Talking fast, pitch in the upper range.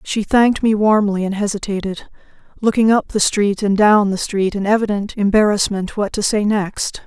No: average, 180 wpm; high, 205 Hz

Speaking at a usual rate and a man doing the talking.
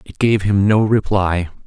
Yes: average, 180 wpm; male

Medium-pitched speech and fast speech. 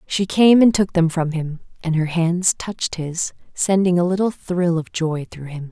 Yes: medium, 175 Hz; fast, 210 wpm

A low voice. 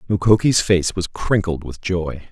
Yes: very low, 95 Hz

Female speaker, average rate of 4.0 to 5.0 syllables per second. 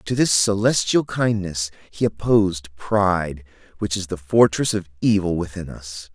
No: male; 4.4 syllables/s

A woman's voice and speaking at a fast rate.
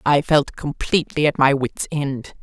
No: female; average, 175 wpm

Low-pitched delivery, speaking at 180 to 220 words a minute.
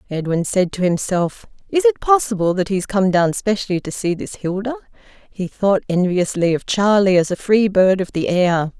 No: high, 195 Hz; average, 200 wpm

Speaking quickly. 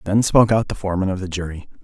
Yes: fast, 260 wpm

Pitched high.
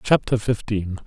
No: low, 110 Hz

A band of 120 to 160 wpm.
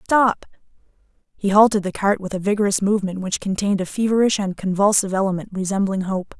No: average, 170 wpm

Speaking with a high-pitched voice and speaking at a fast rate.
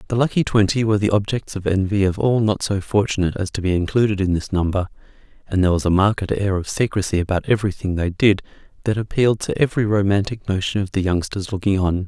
No: low, 100 Hz; fast, 215 wpm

